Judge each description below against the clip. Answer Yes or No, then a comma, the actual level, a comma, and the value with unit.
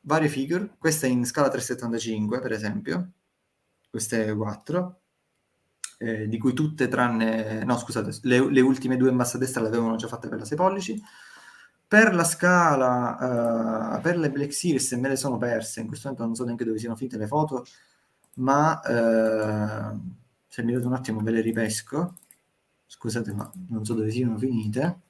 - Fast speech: Yes, fast, 175 wpm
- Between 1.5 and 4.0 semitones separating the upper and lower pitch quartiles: No, average, 4.6 semitones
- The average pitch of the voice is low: Yes, low, 125 Hz